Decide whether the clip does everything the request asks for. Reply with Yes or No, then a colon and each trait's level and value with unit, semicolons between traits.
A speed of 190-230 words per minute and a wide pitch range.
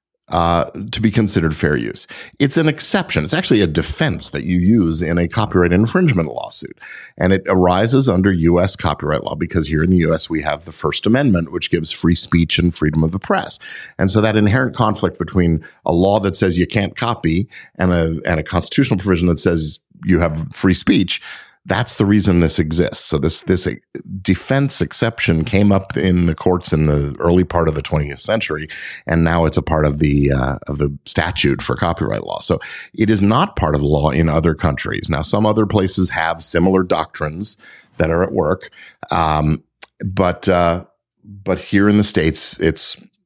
No: average, 195 wpm; average, 4.0 semitones